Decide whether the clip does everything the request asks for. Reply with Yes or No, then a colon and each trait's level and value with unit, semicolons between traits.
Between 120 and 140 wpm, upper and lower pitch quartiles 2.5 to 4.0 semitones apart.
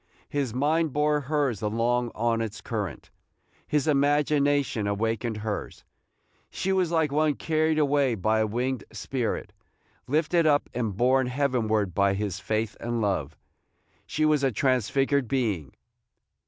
No: slow, 135 wpm; average, 5.0 semitones